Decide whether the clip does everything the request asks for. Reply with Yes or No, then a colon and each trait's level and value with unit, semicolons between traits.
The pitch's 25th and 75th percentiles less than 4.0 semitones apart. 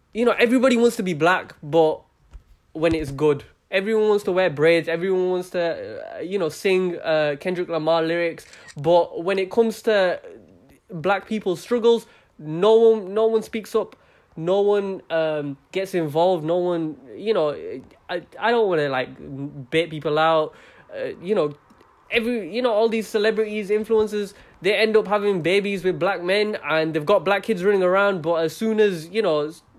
No: average, 4.9 semitones